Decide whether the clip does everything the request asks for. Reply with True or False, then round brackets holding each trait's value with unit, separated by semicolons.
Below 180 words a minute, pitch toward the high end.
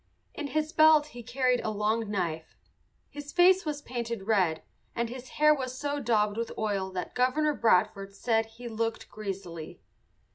True (160 wpm; 230 Hz)